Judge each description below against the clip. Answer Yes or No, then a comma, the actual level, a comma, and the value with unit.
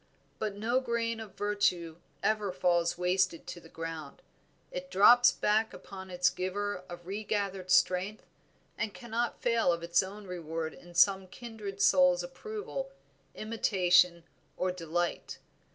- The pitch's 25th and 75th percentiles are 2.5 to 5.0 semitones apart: Yes, average, 3.7 semitones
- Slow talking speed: Yes, slow, 130 wpm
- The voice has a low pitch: No, high, 190 Hz